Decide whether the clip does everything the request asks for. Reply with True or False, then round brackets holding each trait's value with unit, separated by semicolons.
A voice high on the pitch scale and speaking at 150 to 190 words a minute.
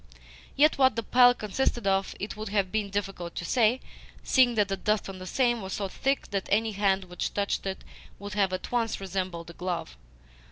False (200 Hz; 205 wpm)